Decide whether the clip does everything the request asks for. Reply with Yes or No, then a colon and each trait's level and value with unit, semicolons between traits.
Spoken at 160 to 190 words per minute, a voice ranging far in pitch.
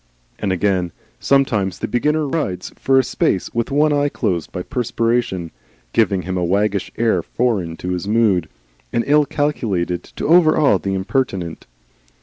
No: average, 150 wpm; wide, 6.7 semitones